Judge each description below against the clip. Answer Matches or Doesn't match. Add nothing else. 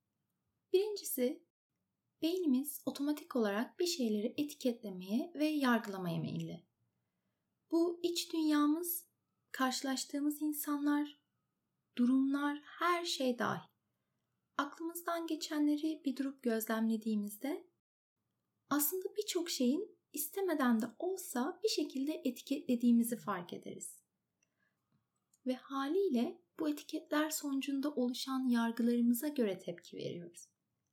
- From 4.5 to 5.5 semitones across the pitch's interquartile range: Matches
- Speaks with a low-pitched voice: Doesn't match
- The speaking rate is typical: Doesn't match